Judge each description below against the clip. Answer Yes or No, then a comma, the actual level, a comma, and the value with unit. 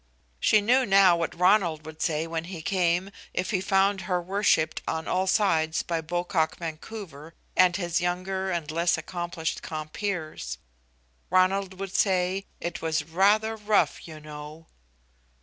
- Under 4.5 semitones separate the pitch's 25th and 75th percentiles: Yes, average, 3.1 semitones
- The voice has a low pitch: No, medium, 175 Hz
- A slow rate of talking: No, average, 145 wpm